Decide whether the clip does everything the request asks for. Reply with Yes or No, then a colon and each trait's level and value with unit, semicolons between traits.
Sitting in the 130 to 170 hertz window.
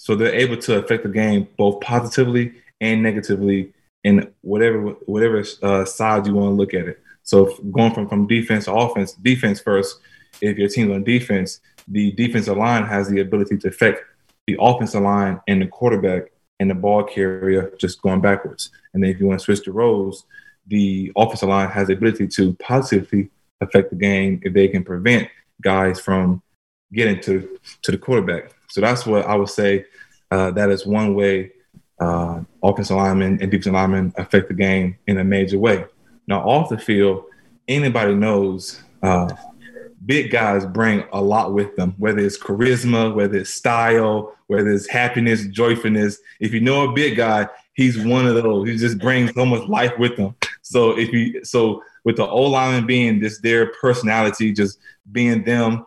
No: low, 105 Hz